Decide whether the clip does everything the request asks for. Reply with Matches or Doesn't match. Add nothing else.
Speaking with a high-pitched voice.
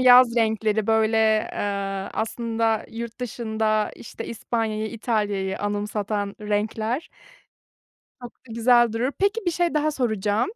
Matches